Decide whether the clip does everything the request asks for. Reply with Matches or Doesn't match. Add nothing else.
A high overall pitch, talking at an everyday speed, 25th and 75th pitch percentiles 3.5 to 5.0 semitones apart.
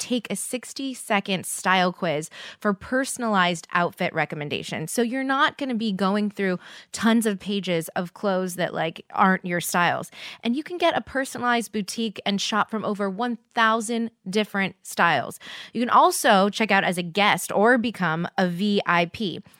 Matches